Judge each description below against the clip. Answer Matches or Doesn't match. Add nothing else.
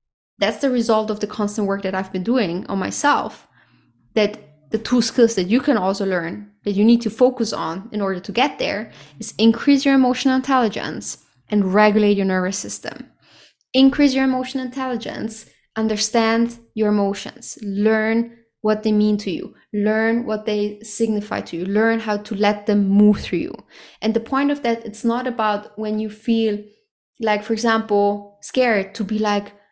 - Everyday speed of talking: Matches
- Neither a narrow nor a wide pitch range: Doesn't match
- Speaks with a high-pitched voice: Matches